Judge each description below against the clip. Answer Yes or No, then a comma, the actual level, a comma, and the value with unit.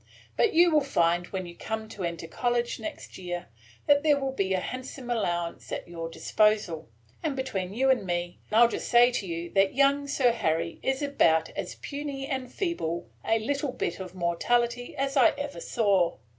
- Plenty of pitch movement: Yes, wide, 7.5 semitones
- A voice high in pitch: Yes, high, 225 Hz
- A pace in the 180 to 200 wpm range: Yes, average, 190 wpm